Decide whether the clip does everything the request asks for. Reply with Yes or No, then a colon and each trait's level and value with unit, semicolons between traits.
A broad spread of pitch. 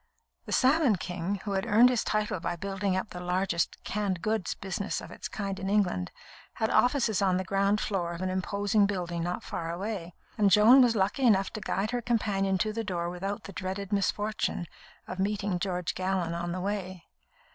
No: narrow, 2.5 semitones